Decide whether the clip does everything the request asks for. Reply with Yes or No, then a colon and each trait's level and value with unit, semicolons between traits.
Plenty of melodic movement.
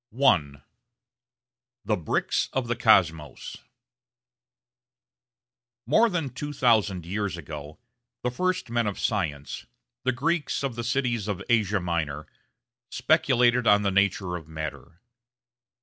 Yes: wide, 6.6 semitones